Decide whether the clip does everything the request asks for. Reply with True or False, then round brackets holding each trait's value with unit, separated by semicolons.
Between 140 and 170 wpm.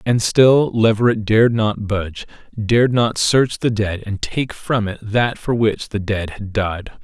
False (190 wpm)